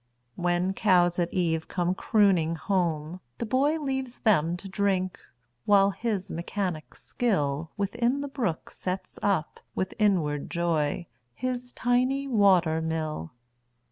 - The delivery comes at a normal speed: No, slow, 110 wpm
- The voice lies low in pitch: No, medium, 185 Hz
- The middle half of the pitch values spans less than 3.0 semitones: No, average, 5.0 semitones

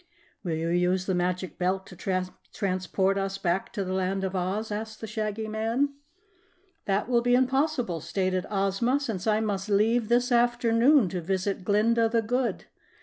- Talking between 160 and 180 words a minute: Yes, average, 165 wpm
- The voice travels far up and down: No, average, 3.6 semitones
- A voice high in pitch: Yes, high, 205 Hz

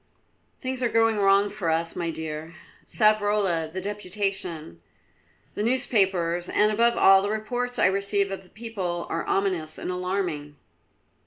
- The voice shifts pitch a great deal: No, average, 3.7 semitones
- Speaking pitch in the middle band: No, high, 195 Hz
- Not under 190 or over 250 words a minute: No, average, 145 wpm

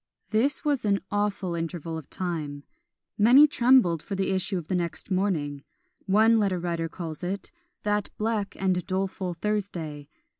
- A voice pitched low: No, high, 190 Hz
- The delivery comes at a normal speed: Yes, average, 150 wpm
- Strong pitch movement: No, average, 3.7 semitones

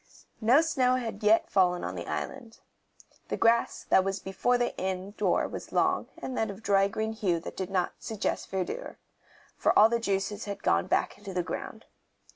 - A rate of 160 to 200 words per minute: Yes, average, 195 wpm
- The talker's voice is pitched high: Yes, high, 205 Hz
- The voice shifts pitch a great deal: No, average, 3.3 semitones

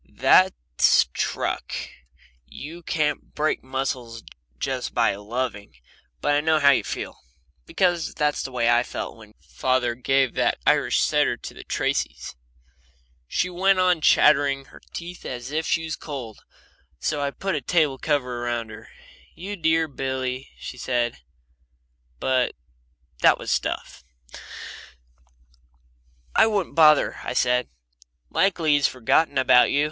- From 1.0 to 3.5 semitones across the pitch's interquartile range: No, average, 4.4 semitones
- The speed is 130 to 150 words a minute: Yes, slow, 135 wpm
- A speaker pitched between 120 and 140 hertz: Yes, low, 135 Hz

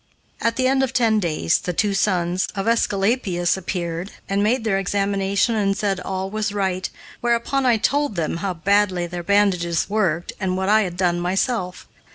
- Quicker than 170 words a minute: Yes, average, 180 wpm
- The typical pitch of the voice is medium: No, high, 195 Hz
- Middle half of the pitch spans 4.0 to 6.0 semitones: No, average, 3.3 semitones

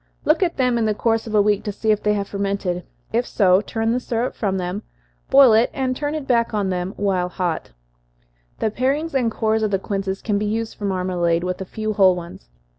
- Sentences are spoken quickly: Yes, fast, 220 wpm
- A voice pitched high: Yes, high, 210 Hz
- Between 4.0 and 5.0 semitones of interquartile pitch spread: No, average, 3.4 semitones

